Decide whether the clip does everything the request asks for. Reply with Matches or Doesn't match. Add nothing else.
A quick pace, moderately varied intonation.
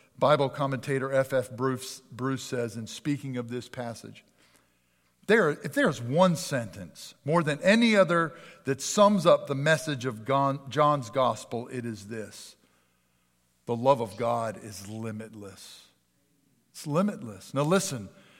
Doesn't match